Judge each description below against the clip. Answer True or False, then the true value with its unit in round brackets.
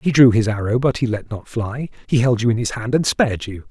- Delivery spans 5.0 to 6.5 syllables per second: True (5.9 syllables/s)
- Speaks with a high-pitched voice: False (120 Hz)